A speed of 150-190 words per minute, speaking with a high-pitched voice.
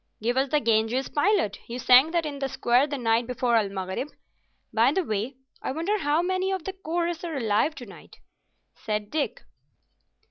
Yes: average, 185 wpm; very high, 270 Hz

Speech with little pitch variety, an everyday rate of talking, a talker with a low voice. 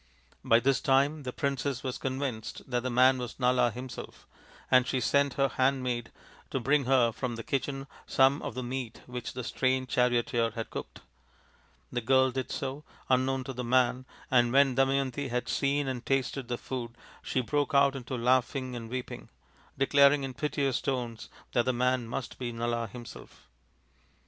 Yes: narrow, 1.8 semitones; average, 170 wpm; low, 130 Hz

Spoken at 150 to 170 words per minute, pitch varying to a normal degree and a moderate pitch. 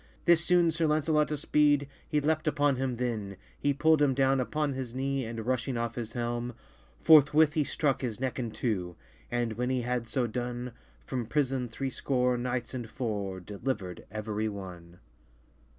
No: average, 165 wpm; average, 3.9 semitones; low, 125 Hz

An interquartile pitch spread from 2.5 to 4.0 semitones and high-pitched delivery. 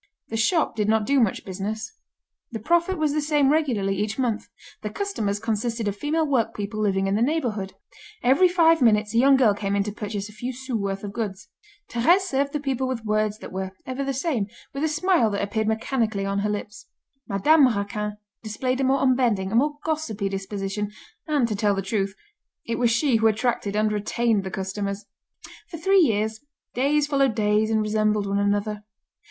No: average, 4.7 semitones; high, 220 Hz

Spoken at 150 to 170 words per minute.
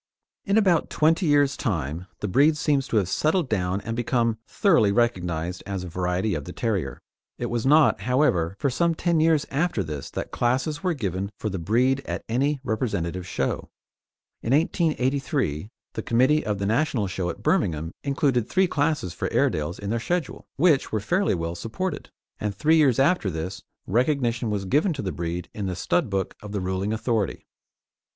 No: average, 180 wpm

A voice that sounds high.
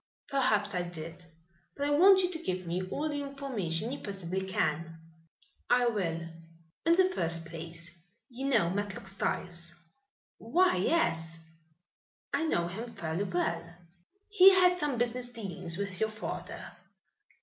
Yes: high, 200 Hz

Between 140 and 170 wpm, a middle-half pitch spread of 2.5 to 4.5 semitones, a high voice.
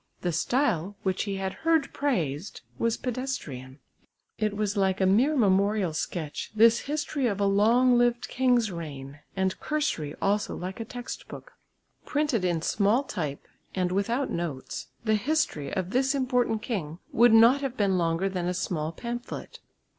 No: average, 160 wpm; wide, 5.5 semitones; high, 205 Hz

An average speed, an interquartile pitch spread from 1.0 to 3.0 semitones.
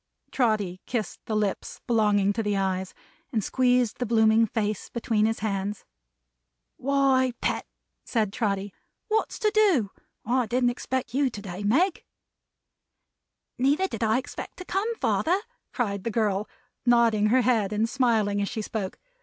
No: average, 150 wpm; average, 3.7 semitones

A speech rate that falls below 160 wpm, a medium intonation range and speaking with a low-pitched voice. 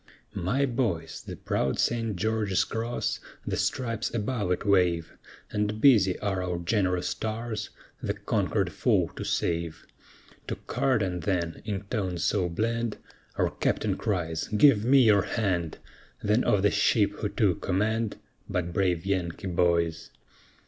Yes: average, 140 wpm; average, 4.1 semitones; low, 100 Hz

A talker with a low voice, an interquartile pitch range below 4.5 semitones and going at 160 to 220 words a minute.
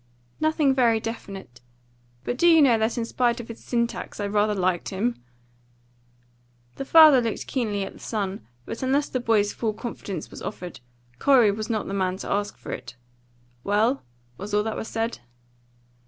No: high, 225 Hz; average, 3.3 semitones; average, 170 wpm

